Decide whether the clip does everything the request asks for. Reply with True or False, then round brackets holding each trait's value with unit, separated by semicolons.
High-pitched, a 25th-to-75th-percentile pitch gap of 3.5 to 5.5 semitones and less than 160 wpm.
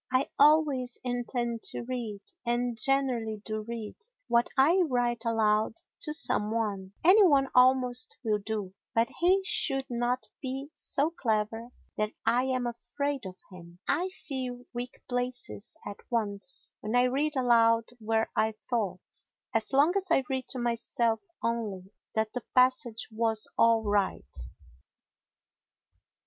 False (240 Hz; 3.0 semitones; 140 wpm)